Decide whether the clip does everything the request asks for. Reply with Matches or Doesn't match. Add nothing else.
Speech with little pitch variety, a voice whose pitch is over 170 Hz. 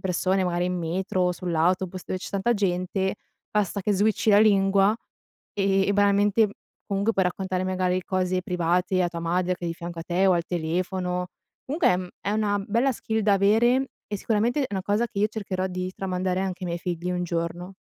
Matches